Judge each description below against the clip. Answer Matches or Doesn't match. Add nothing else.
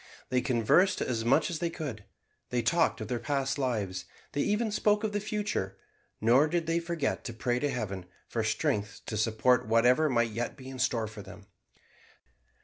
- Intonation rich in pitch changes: Matches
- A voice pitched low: Matches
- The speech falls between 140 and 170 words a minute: Doesn't match